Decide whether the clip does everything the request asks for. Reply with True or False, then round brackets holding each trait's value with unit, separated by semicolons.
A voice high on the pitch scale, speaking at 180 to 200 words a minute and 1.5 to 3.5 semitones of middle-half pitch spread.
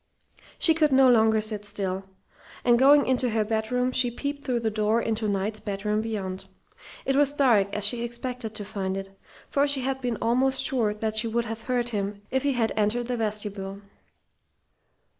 True (225 Hz; 185 wpm; 3.2 semitones)